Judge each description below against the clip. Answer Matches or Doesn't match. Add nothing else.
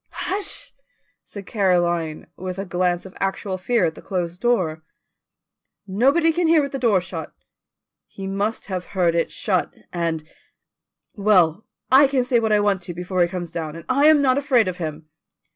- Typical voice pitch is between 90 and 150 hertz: Doesn't match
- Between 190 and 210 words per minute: Doesn't match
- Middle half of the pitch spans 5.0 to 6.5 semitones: Matches